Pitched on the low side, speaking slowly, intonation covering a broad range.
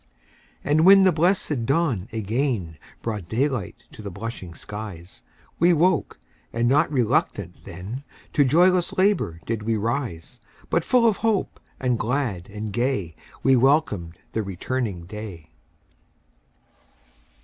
Yes: low, 120 Hz; slow, 125 wpm; wide, 6.9 semitones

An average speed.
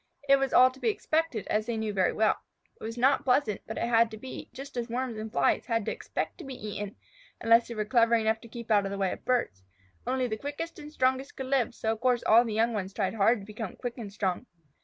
No: fast, 265 wpm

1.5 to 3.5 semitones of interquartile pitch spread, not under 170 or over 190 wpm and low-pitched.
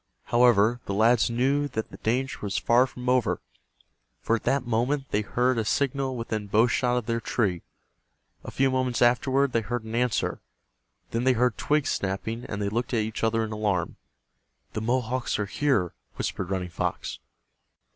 Yes: average, 2.9 semitones; average, 175 wpm; low, 120 Hz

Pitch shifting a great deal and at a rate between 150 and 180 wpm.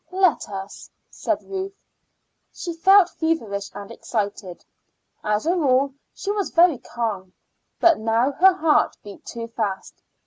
No: wide, 8.9 semitones; slow, 135 wpm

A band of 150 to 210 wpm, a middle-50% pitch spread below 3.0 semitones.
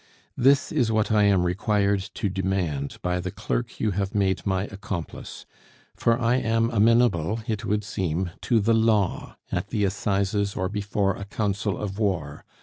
Yes: average, 165 wpm; narrow, 2.5 semitones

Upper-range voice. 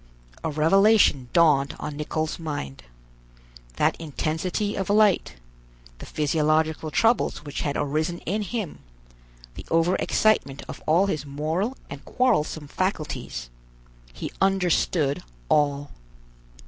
No: medium, 155 Hz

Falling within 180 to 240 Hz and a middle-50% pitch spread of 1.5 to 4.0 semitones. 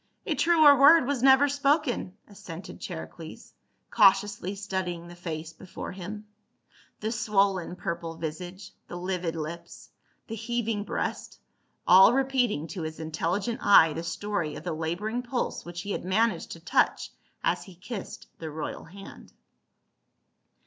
No: high, 190 Hz; average, 5.1 semitones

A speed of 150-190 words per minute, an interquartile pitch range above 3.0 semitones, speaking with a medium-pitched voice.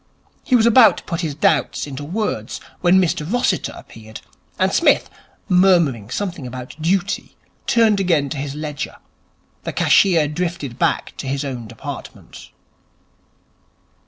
No: slow, 135 wpm; wide, 5.5 semitones; medium, 160 Hz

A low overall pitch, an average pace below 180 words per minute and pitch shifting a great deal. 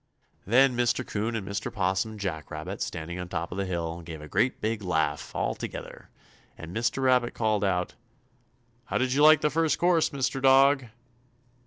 No: low, 110 Hz; average, 185 wpm; wide, 6.6 semitones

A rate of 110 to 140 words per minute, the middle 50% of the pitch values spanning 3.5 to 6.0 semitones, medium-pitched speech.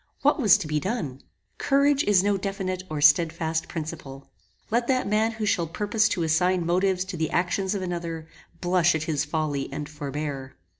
No: average, 180 wpm; average, 4.3 semitones; medium, 175 Hz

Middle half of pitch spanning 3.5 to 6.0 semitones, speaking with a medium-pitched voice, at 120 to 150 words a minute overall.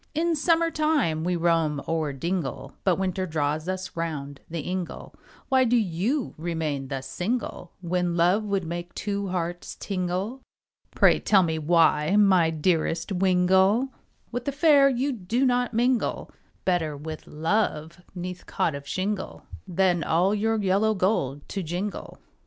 Yes: average, 4.5 semitones; medium, 180 Hz; average, 145 wpm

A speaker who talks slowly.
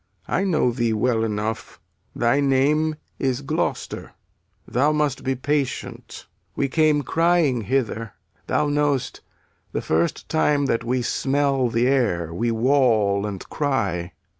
Yes: slow, 130 wpm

